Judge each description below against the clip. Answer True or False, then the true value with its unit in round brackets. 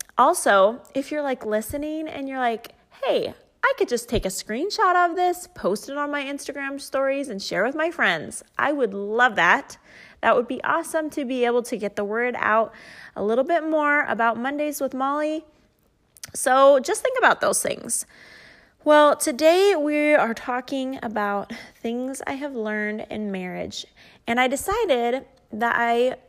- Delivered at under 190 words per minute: True (170 wpm)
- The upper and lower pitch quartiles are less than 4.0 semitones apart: False (4.6 semitones)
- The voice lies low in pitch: False (270 Hz)